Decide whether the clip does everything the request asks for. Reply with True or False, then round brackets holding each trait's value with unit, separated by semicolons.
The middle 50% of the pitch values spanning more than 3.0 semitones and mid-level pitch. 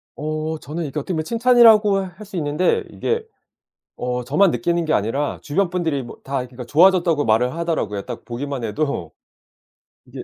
True (5.3 semitones; 155 Hz)